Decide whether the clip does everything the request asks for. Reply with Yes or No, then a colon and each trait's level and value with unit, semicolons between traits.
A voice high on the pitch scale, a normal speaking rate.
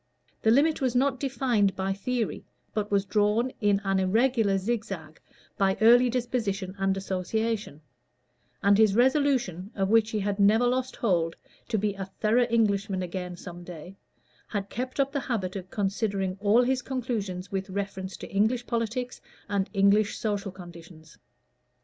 Yes: high, 205 Hz; average, 155 wpm